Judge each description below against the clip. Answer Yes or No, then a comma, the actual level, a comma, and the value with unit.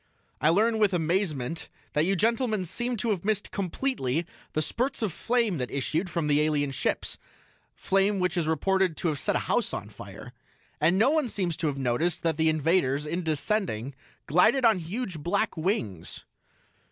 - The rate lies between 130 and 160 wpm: No, average, 175 wpm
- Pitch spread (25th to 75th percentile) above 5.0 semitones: Yes, wide, 5.5 semitones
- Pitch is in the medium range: Yes, medium, 175 Hz